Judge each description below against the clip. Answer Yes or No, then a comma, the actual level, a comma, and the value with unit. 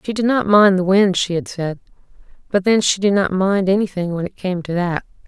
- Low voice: No, high, 190 Hz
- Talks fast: Yes, fast, 240 wpm